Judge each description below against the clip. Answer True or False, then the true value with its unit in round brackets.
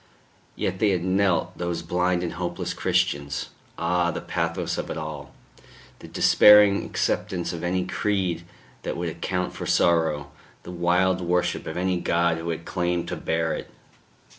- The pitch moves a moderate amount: False (1.6 semitones)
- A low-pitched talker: True (85 Hz)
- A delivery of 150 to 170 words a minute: True (160 wpm)